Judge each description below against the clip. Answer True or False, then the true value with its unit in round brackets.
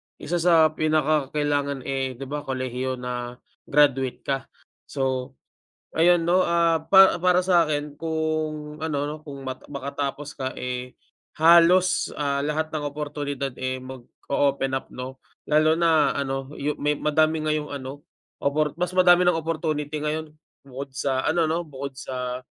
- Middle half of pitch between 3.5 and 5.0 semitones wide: False (2.8 semitones)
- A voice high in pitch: False (150 Hz)